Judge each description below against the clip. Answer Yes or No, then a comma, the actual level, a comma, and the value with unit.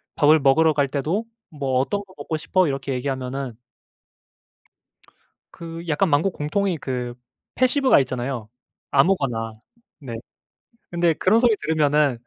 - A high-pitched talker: No, medium, 150 Hz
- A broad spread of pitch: No, average, 4.4 semitones